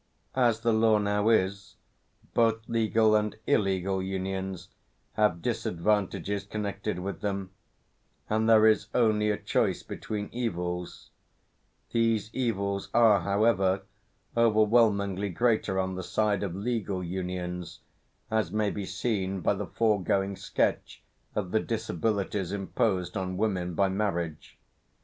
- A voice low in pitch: Yes, low, 100 Hz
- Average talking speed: No, slow, 120 wpm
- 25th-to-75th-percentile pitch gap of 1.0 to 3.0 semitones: Yes, narrow, 2.6 semitones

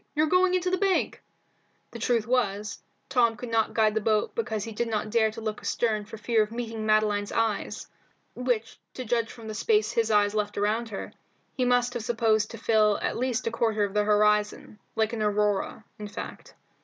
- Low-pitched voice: No, high, 220 Hz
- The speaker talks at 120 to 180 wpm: No, fast, 205 wpm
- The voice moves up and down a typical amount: No, narrow, 2.1 semitones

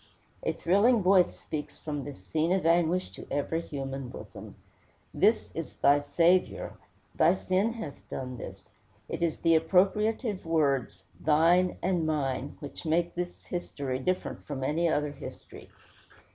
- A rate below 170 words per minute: Yes, average, 145 wpm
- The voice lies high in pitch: No, medium, 160 Hz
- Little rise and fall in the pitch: No, average, 4.1 semitones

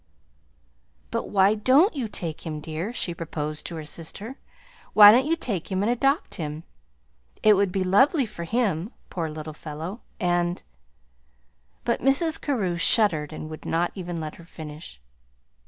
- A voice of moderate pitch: Yes, medium, 175 Hz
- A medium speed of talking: Yes, average, 160 wpm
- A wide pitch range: Yes, wide, 6.0 semitones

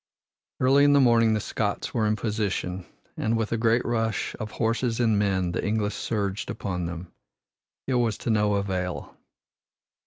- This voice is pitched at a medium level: No, low, 110 Hz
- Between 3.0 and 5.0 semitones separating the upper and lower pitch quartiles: No, narrow, 2.6 semitones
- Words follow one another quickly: No, average, 165 wpm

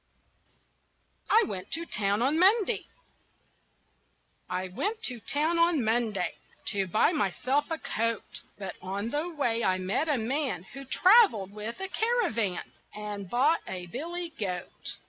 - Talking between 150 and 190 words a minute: No, average, 140 wpm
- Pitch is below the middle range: No, high, 240 Hz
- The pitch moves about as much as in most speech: No, wide, 8.5 semitones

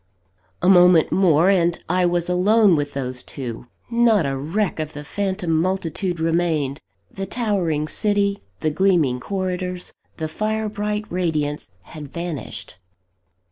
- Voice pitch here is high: No, medium, 175 Hz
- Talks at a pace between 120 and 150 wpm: Yes, slow, 135 wpm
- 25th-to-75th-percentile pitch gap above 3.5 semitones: Yes, average, 4.2 semitones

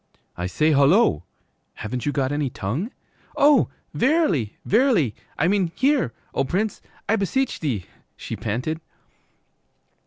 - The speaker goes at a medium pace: No, slow, 120 wpm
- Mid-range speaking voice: Yes, medium, 160 Hz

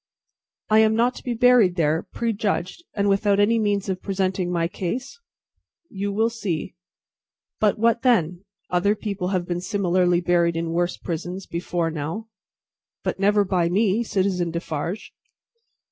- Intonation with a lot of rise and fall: No, average, 3.4 semitones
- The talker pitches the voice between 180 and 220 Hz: Yes, high, 190 Hz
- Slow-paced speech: No, average, 145 wpm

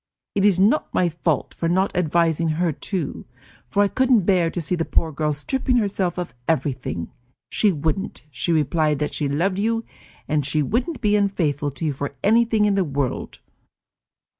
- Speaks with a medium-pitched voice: Yes, medium, 170 Hz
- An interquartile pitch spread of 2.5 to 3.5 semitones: No, average, 5.1 semitones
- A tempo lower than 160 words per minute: No, average, 180 wpm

